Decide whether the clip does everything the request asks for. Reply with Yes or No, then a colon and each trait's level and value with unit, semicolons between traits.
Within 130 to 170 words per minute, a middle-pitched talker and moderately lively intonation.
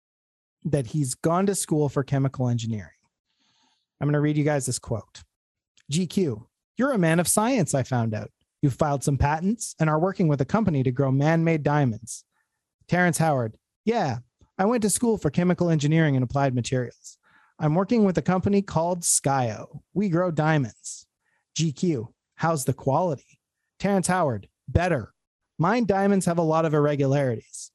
Yes: average, 165 wpm; medium, 155 Hz; average, 4.9 semitones